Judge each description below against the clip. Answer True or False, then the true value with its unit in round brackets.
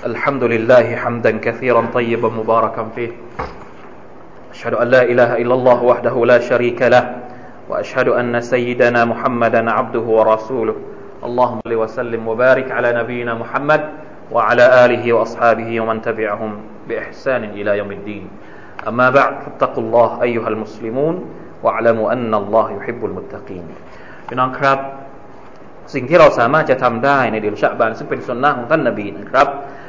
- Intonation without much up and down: True (1.7 semitones)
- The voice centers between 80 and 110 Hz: False (120 Hz)